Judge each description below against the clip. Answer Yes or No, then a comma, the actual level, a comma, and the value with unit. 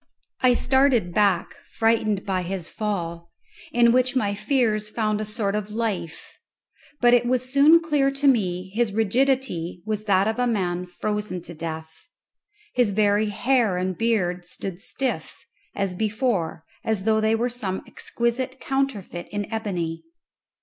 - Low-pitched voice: No, high, 215 Hz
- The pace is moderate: Yes, average, 150 wpm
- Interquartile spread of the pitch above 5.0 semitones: No, average, 4.5 semitones